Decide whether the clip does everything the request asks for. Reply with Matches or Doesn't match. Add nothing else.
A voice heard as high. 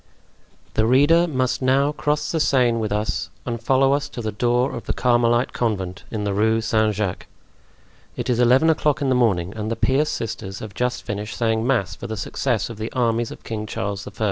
Doesn't match